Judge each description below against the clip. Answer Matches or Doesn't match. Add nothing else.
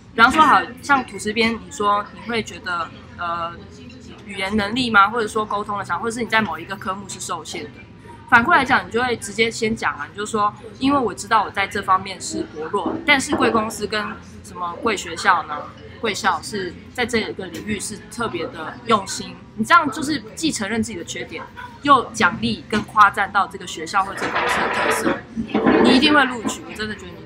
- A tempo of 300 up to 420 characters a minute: Matches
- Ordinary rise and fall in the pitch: Matches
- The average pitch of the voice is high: Matches